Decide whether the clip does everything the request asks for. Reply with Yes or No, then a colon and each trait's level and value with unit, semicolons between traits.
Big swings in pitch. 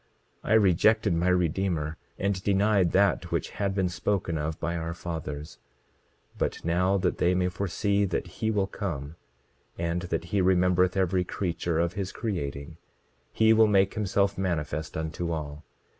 No: average, 2.9 semitones